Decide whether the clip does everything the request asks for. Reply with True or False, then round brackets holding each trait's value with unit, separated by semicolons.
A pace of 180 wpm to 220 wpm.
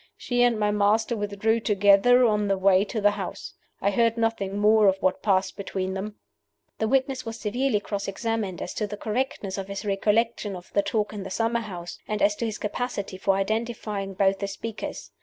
True (200 wpm)